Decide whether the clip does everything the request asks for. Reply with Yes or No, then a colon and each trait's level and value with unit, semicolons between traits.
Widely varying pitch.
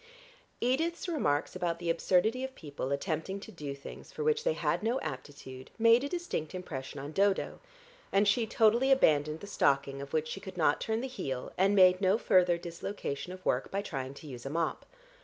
Yes: wide, 7.3 semitones